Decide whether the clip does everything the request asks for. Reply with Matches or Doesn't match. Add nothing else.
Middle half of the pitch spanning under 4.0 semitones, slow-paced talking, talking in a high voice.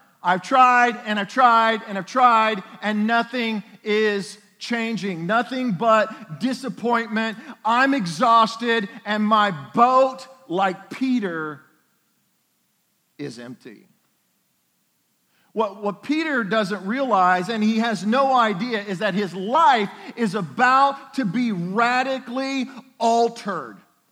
Matches